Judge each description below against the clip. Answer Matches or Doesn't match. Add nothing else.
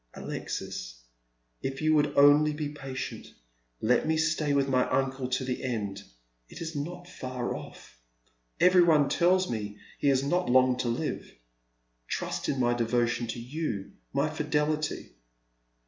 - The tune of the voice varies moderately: Matches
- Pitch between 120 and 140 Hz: Matches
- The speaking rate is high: Doesn't match